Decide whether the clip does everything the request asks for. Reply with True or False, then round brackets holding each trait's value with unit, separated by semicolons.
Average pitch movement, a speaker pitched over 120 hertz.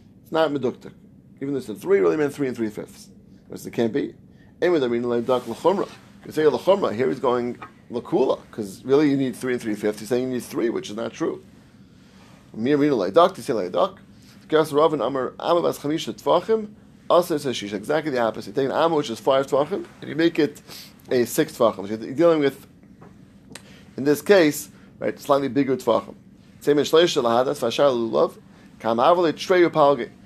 True (4.7 semitones; 135 Hz)